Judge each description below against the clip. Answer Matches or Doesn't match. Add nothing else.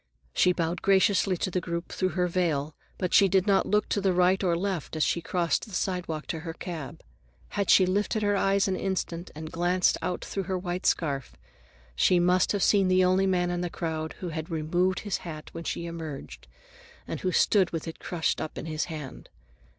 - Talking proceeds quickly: Matches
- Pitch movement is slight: Matches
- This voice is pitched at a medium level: Matches